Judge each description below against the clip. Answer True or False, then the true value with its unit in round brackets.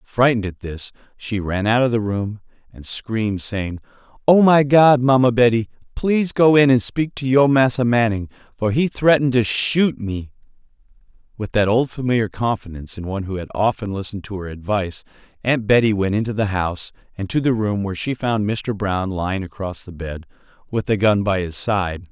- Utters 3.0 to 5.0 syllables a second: False (5.4 syllables/s)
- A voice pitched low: True (110 Hz)